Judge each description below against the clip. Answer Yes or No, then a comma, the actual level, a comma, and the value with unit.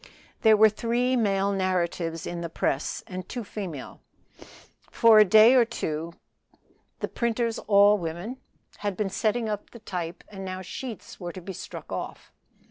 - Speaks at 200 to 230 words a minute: No, average, 170 wpm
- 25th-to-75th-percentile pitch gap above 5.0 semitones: No, average, 3.9 semitones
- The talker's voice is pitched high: Yes, high, 200 Hz